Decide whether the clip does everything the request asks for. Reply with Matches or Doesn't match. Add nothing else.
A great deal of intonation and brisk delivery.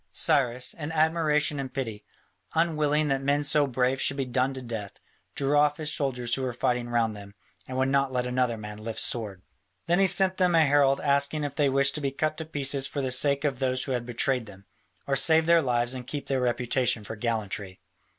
Doesn't match